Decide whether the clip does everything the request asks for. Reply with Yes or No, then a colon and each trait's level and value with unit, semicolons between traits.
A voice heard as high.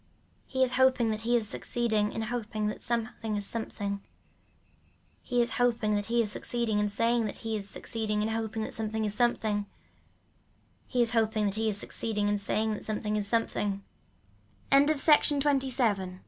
Yes: high, 220 Hz